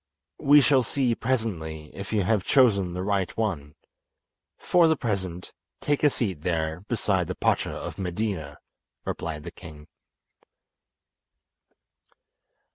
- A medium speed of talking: No, slow, 125 wpm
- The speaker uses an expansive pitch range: Yes, wide, 5.8 semitones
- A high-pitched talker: No, very low, 95 Hz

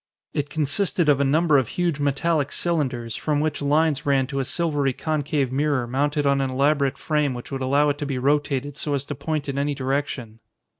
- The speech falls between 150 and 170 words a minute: No, fast, 205 wpm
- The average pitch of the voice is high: No, medium, 145 Hz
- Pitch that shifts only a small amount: Yes, narrow, 1.8 semitones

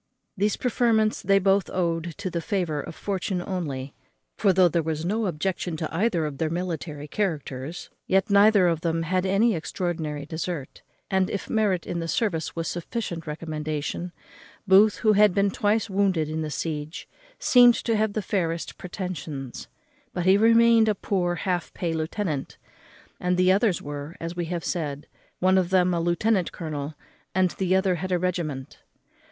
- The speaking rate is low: No, average, 170 wpm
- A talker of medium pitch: Yes, medium, 180 Hz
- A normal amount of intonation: Yes, average, 3.5 semitones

